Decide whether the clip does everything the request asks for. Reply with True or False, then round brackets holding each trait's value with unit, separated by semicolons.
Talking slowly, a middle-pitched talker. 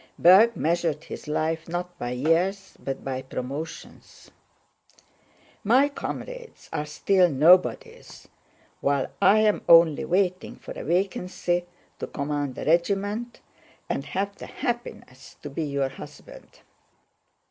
True (120 wpm; 175 Hz)